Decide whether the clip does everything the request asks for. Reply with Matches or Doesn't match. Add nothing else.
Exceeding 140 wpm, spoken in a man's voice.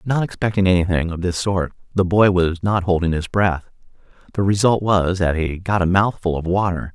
Matches